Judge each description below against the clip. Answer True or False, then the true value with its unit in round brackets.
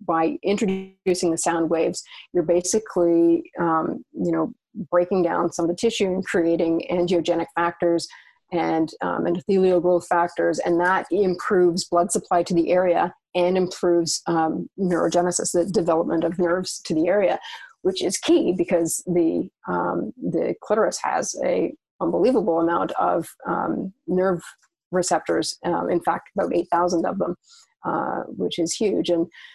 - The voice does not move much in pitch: True (1.5 semitones)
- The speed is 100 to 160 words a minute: True (150 wpm)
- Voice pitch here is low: False (175 Hz)